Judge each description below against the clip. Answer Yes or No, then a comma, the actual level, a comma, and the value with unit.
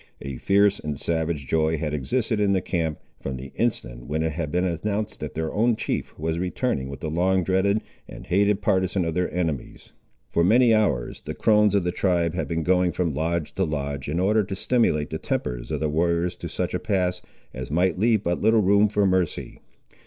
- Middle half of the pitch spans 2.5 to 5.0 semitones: Yes, average, 4.4 semitones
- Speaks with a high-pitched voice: No, very low, 90 Hz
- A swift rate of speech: Yes, fast, 210 wpm